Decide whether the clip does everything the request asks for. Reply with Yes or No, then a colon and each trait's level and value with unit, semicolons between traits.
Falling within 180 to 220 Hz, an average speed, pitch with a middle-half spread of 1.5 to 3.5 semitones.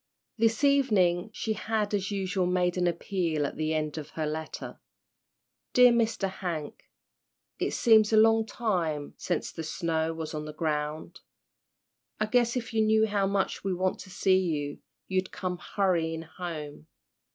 No: medium, 185 Hz; average, 160 wpm; average, 5.1 semitones